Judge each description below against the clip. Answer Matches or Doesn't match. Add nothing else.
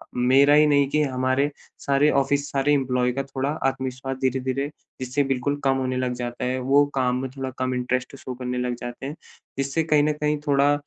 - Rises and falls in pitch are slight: Matches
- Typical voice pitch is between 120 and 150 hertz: Matches